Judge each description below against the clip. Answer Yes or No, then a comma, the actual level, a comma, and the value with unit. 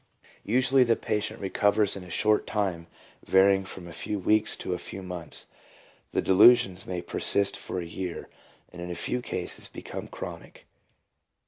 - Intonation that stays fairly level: No, average, 3.0 semitones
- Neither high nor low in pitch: No, very low, 95 Hz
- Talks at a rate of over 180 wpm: No, average, 160 wpm